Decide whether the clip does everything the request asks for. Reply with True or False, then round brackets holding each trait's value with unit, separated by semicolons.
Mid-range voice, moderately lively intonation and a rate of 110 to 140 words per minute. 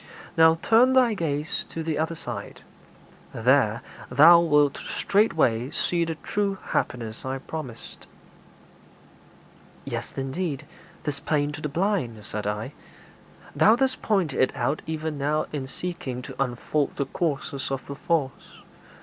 True (150 Hz; 4.1 semitones; 135 wpm)